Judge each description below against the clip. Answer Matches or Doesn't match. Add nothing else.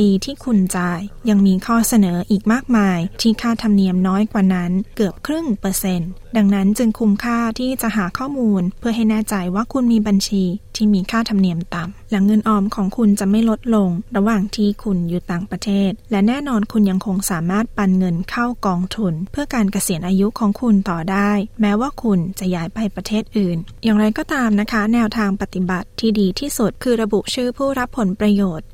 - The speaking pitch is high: Matches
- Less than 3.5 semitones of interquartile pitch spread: Matches